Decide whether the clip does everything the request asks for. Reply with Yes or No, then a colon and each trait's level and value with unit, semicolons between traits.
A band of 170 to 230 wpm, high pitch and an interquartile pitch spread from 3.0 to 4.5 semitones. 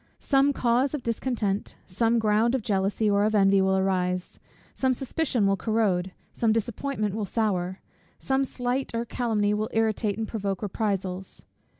No: average, 155 wpm; high, 215 Hz; average, 3.4 semitones